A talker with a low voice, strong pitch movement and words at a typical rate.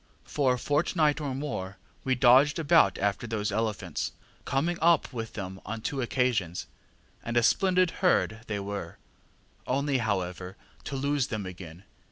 Yes: low, 120 Hz; wide, 6.1 semitones; average, 150 wpm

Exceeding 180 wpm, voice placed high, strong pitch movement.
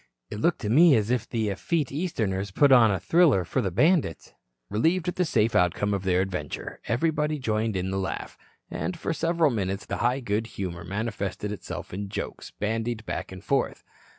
No: average, 190 wpm; low, 110 Hz; wide, 6.6 semitones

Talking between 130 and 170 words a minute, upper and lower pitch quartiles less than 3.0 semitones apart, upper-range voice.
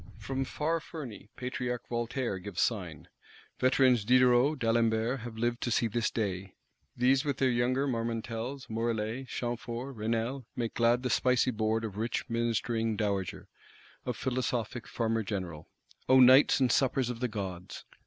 No: average, 145 wpm; narrow, 2.4 semitones; low, 120 Hz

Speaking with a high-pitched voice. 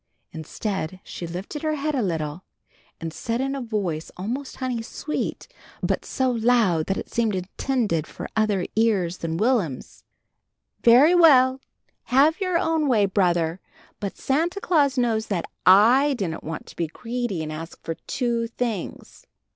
Yes: high, 225 Hz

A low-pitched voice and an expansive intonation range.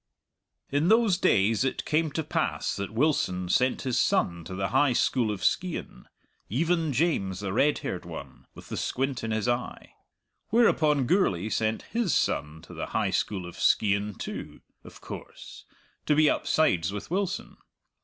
Yes: low, 125 Hz; wide, 7.9 semitones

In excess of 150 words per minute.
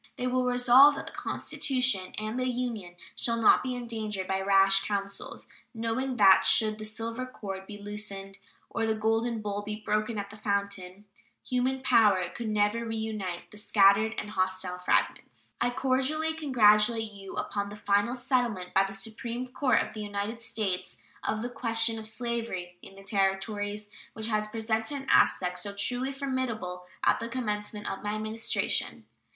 Yes: average, 165 wpm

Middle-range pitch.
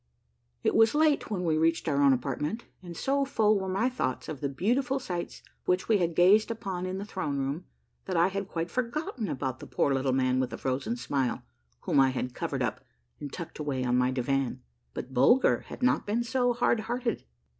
Yes: medium, 180 Hz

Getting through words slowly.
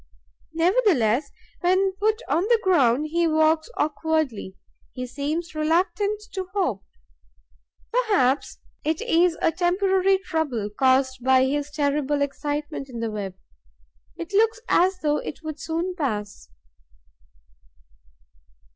Yes: slow, 115 wpm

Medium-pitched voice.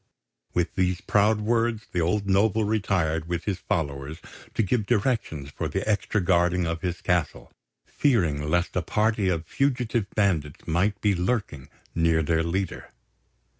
No: very low, 90 Hz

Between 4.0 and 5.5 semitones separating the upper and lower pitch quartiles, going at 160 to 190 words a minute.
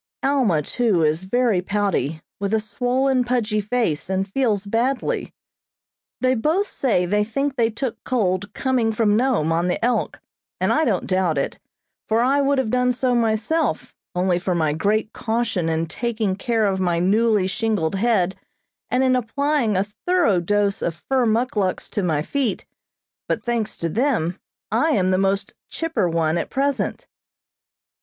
Yes: average, 5.2 semitones; average, 165 wpm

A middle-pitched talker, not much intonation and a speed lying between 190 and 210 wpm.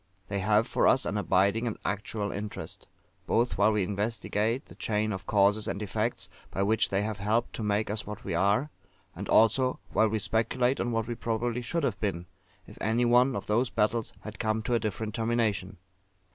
No: low, 110 Hz; narrow, 2.2 semitones; average, 200 wpm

